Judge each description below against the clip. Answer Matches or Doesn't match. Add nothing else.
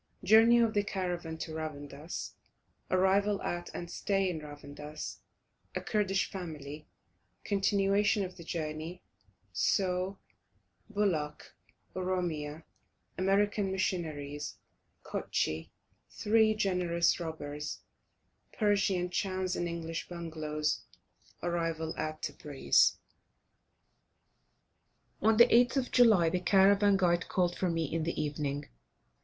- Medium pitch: Matches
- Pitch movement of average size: Matches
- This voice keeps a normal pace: Doesn't match